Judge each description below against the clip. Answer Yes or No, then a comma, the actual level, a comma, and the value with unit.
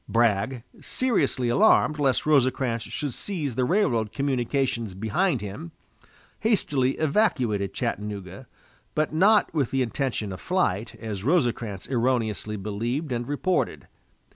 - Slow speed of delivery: Yes, slow, 115 wpm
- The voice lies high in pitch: No, low, 125 Hz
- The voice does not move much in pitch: No, average, 5.3 semitones